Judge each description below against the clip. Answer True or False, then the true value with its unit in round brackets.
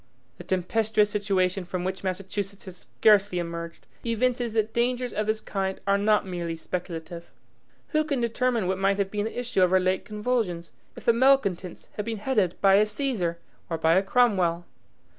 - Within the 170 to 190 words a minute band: True (180 wpm)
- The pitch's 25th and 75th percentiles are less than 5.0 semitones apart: True (3.6 semitones)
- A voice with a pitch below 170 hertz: False (200 Hz)